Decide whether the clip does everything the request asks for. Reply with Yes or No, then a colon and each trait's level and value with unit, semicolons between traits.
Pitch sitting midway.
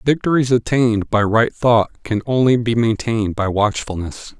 No: low, 115 Hz